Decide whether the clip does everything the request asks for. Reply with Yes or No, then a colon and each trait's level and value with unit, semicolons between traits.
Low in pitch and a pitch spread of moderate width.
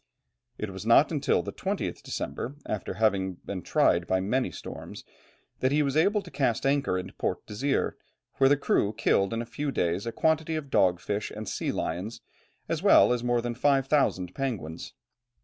No: low, 120 Hz; wide, 6.5 semitones